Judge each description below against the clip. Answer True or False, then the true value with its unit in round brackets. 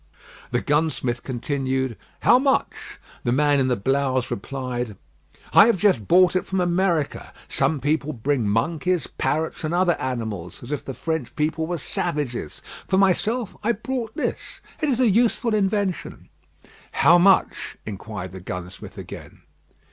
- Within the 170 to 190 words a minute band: False (150 wpm)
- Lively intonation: True (6.8 semitones)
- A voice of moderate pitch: True (150 Hz)